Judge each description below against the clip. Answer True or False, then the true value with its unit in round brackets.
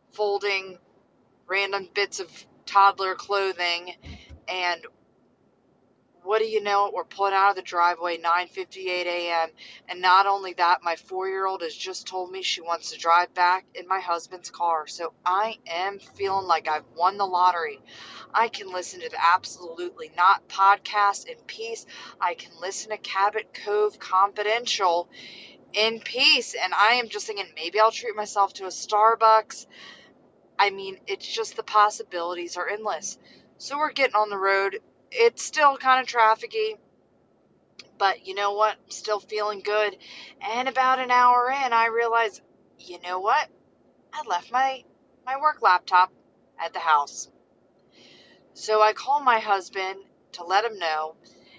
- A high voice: True (200 Hz)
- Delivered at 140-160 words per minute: True (155 wpm)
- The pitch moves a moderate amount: True (4.4 semitones)